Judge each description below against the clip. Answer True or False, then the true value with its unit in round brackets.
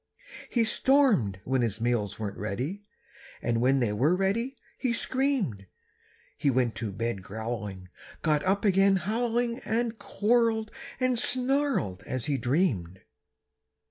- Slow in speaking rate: True (130 wpm)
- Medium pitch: True (155 Hz)